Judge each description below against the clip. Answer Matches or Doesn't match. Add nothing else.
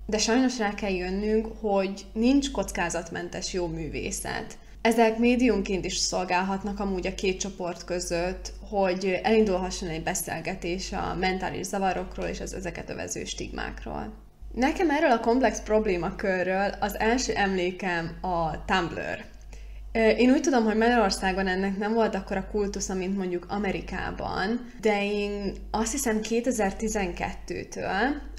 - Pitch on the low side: Doesn't match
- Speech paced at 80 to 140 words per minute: Matches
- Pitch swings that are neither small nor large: Matches